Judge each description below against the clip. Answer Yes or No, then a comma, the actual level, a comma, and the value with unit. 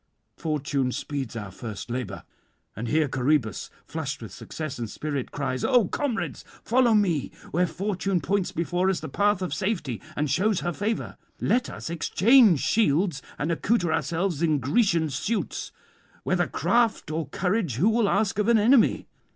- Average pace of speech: Yes, average, 160 wpm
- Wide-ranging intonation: Yes, wide, 6.6 semitones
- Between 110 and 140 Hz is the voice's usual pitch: No, medium, 170 Hz